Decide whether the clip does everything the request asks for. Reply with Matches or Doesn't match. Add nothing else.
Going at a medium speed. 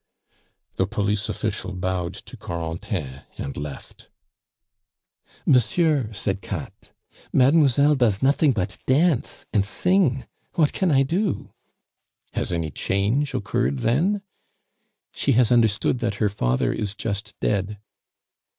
Doesn't match